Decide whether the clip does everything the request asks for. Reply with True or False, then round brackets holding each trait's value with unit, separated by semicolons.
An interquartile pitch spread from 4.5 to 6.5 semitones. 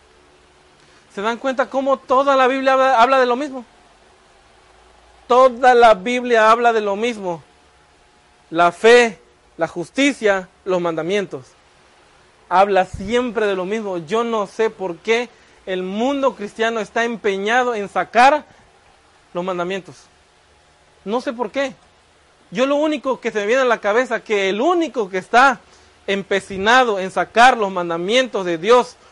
True (5.2 semitones)